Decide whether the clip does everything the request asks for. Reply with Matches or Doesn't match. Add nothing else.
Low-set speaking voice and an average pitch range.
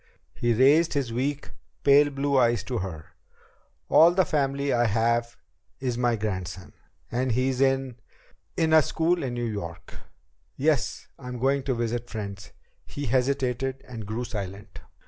Matches